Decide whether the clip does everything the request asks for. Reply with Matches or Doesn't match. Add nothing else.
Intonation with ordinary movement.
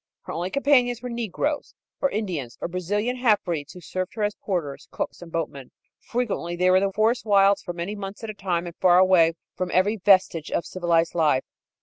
Matches